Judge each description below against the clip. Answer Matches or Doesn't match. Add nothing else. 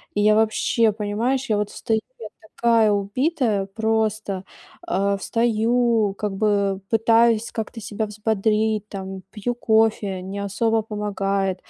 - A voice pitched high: Matches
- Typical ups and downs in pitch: Doesn't match